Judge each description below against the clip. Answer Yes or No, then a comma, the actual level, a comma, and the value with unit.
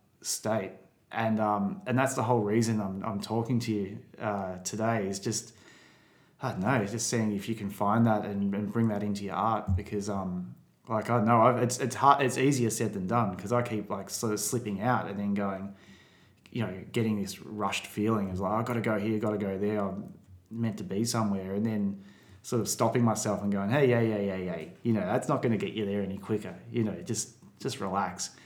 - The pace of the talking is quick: Yes, fast, 235 wpm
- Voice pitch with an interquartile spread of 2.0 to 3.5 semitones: Yes, narrow, 2.4 semitones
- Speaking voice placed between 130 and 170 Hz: No, low, 105 Hz